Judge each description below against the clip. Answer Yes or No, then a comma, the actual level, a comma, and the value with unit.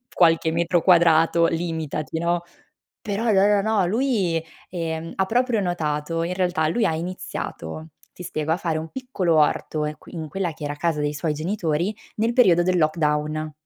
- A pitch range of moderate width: Yes, average, 3.0 semitones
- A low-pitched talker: No, medium, 170 Hz